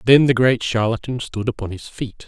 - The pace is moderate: No, fast, 210 wpm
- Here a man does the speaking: Yes, male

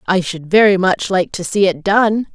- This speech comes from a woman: Yes, female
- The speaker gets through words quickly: Yes, fast, 230 wpm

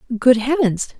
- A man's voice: No, female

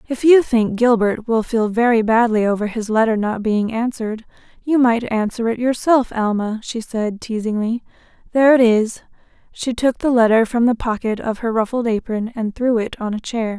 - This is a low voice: No, high, 230 Hz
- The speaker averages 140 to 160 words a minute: No, average, 185 wpm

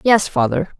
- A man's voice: No, female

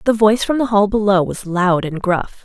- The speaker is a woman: Yes, female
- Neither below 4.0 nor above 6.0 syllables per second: Yes, 5.2 syllables/s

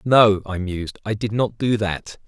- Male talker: Yes, male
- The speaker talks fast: Yes, fast, 210 wpm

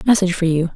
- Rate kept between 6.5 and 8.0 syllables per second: No, 8.2 syllables/s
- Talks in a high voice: No, medium, 180 Hz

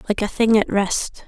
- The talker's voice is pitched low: No, high, 210 Hz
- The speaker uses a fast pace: Yes, fast, 235 wpm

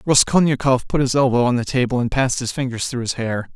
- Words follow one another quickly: Yes, fast, 235 wpm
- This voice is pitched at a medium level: No, low, 125 Hz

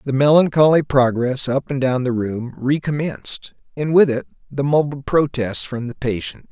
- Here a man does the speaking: Yes, male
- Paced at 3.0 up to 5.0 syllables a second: Yes, 4.8 syllables/s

